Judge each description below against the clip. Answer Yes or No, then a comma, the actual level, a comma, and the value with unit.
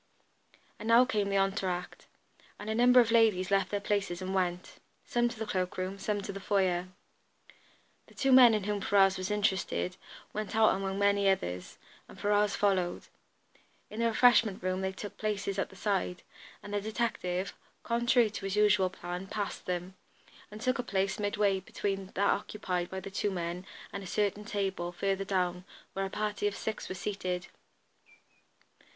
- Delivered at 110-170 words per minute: No, average, 180 wpm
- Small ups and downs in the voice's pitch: Yes, narrow, 2.0 semitones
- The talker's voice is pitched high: Yes, high, 195 Hz